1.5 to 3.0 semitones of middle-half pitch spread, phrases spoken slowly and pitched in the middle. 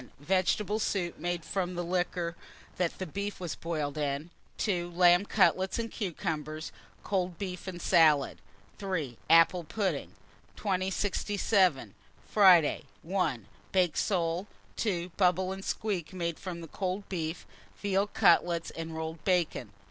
Yes: narrow, 2.6 semitones; slow, 120 wpm; medium, 180 Hz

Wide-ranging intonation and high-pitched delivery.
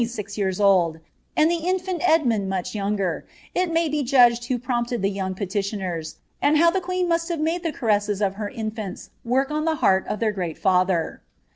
Yes: wide, 7.9 semitones; high, 225 Hz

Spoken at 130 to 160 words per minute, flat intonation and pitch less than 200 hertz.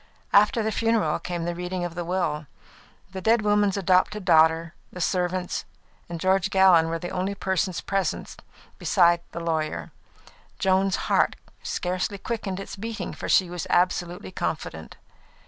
Yes: average, 145 wpm; narrow, 2.3 semitones; medium, 185 Hz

